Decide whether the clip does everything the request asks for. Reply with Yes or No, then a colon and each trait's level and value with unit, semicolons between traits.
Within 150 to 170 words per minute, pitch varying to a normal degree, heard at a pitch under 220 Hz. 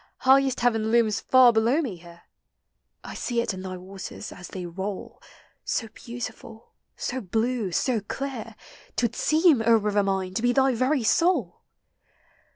No: average, 160 wpm; average, 4.6 semitones; high, 225 Hz